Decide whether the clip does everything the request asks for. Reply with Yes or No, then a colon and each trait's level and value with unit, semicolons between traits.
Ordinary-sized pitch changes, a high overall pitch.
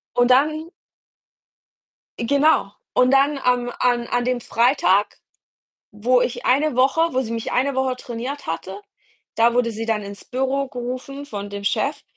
Yes: average, 3.0 semitones; very high, 250 Hz